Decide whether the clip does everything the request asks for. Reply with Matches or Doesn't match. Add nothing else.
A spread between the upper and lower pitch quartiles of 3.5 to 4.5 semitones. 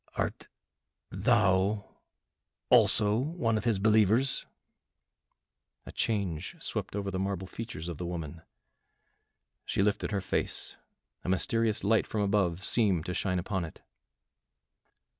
Doesn't match